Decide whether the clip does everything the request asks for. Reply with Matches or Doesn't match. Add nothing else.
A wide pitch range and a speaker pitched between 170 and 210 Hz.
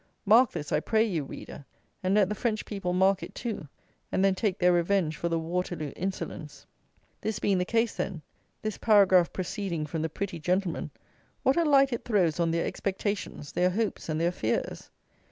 Doesn't match